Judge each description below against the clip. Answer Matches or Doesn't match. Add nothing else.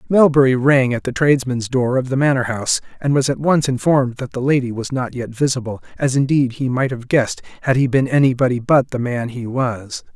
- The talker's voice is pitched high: Doesn't match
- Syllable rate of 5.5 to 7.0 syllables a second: Matches